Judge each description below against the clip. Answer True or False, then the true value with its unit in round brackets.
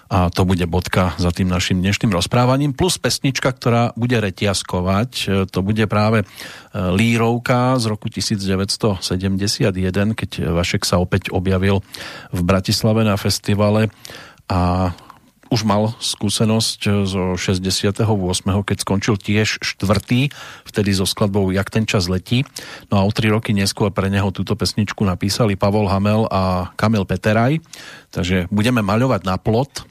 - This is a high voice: False (105 Hz)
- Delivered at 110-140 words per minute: True (135 wpm)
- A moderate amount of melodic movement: True (3.0 semitones)